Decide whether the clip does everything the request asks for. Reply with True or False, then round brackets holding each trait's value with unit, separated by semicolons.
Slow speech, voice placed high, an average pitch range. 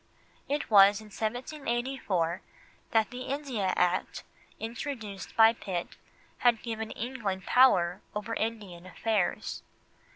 True (105 wpm; 220 Hz; 3.9 semitones)